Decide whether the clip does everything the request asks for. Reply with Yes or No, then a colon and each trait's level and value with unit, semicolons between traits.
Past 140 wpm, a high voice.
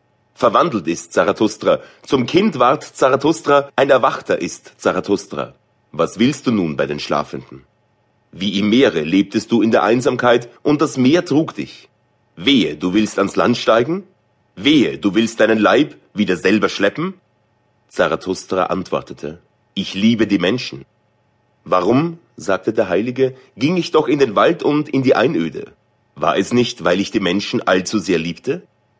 No: average, 155 wpm; low, 115 Hz